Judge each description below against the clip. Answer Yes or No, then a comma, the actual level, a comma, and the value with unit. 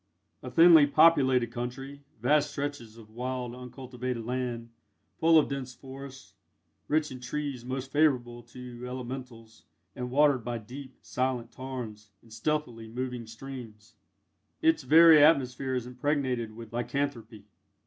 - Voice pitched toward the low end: Yes, low, 125 Hz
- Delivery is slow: Yes, slow, 130 wpm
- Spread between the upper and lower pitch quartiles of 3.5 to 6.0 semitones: No, average, 2.7 semitones